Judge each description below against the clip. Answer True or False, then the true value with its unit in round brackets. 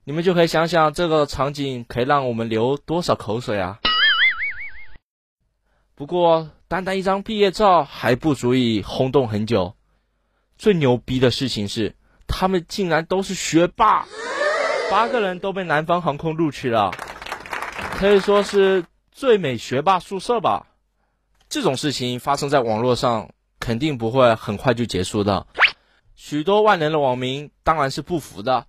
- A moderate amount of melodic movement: False (7.0 semitones)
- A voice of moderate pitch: True (145 Hz)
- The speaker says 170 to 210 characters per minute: False (230 characters per minute)